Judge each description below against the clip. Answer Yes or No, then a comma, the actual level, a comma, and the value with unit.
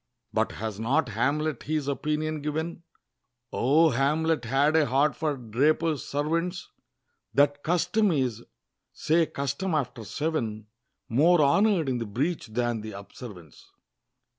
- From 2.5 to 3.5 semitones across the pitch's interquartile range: No, average, 4.6 semitones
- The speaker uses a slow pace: Yes, slow, 125 wpm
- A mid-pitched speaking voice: Yes, medium, 145 Hz